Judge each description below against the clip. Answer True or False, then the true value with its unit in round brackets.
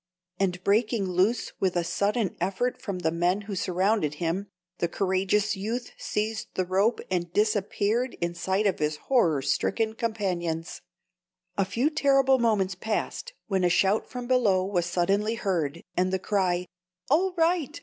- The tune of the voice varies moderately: True (3.8 semitones)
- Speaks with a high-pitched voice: True (195 Hz)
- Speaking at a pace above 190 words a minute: False (155 wpm)